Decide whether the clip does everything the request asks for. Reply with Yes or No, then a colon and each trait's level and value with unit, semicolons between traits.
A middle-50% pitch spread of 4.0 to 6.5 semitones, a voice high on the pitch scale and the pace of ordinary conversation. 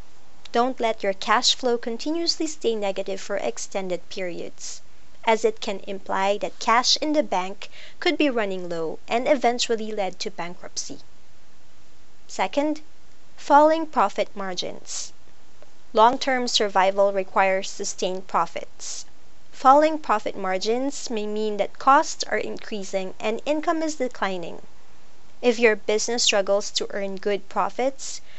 No: average, 4.8 semitones; high, 220 Hz; slow, 125 wpm